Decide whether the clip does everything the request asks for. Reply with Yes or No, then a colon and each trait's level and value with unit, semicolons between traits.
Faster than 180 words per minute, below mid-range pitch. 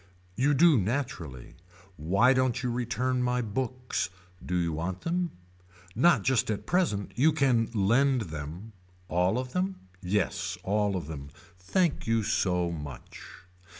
No: average, 140 wpm; low, 115 Hz